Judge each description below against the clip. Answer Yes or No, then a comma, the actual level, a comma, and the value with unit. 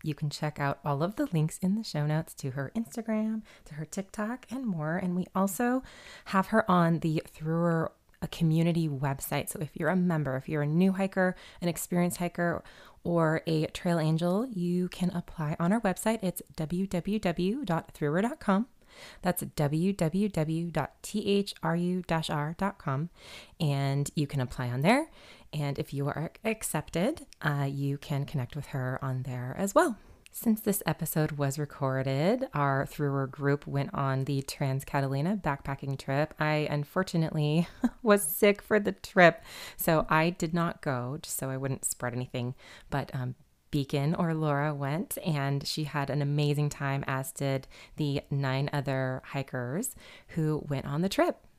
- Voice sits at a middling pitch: Yes, medium, 160 Hz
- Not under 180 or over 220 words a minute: No, average, 155 wpm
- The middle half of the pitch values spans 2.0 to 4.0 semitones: No, average, 4.5 semitones